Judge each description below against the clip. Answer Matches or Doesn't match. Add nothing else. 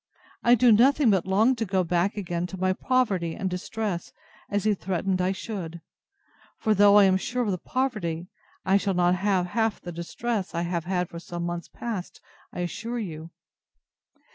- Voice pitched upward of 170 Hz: Matches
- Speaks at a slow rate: Doesn't match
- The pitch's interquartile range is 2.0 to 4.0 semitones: Matches